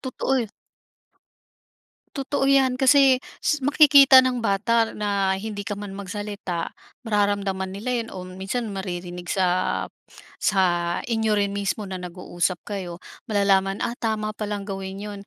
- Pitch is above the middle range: Yes, high, 205 Hz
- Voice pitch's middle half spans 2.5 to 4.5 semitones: Yes, average, 3.2 semitones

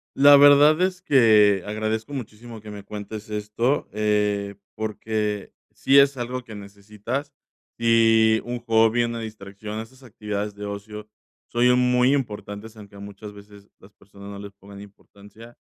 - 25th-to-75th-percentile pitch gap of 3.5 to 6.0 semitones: No, average, 2.7 semitones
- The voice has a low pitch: Yes, low, 110 Hz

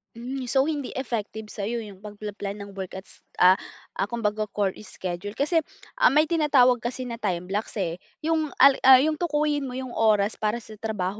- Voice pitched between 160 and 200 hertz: No, high, 225 Hz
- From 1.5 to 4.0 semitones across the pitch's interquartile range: No, average, 4.6 semitones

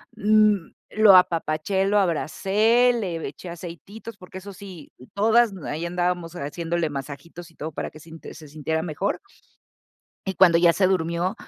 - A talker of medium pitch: Yes, medium, 175 Hz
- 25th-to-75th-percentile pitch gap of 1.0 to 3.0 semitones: No, average, 3.5 semitones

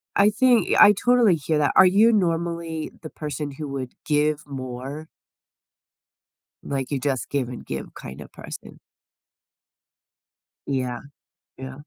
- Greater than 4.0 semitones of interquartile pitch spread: Yes, average, 4.4 semitones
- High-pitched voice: No, medium, 150 Hz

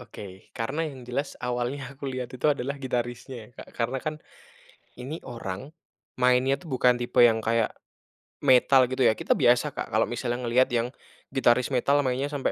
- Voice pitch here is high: No, low, 125 Hz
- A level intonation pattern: Yes, narrow, 2.0 semitones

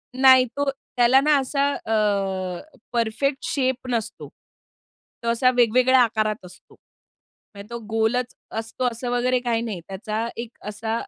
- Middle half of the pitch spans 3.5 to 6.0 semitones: No, average, 2.8 semitones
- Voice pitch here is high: Yes, high, 235 Hz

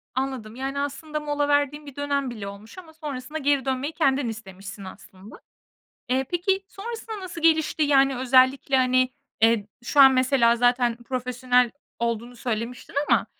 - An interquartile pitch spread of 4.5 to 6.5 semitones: No, average, 3.3 semitones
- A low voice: No, very high, 260 Hz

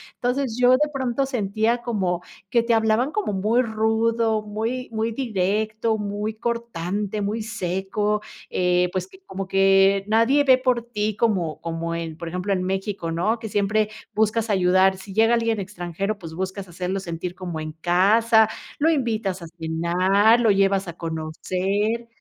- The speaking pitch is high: Yes, high, 210 Hz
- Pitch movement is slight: No, average, 3.6 semitones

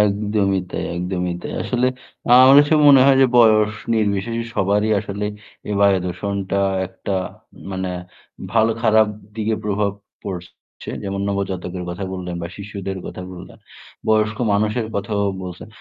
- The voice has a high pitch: No, low, 100 Hz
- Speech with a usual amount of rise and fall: No, narrow, 2.3 semitones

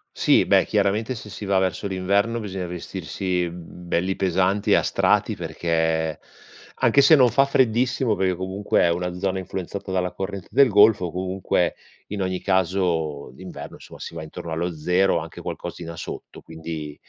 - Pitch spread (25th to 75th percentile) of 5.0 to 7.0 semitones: No, average, 2.8 semitones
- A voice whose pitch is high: No, very low, 95 Hz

